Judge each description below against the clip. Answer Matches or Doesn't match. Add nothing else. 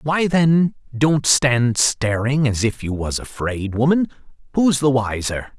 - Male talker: Matches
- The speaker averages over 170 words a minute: Doesn't match